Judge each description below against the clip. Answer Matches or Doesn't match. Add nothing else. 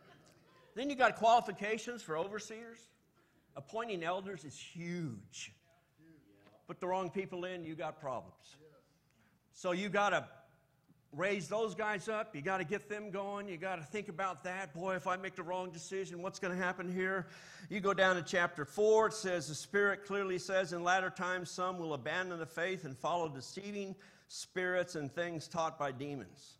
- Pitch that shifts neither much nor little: Matches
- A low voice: Doesn't match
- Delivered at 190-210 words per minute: Doesn't match